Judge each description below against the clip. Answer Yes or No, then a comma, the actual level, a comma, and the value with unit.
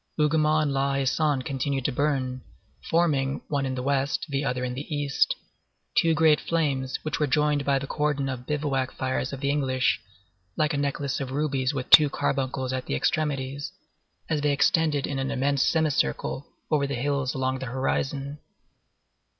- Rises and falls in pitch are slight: Yes, narrow, 2.1 semitones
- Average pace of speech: Yes, average, 175 wpm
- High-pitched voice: No, medium, 140 Hz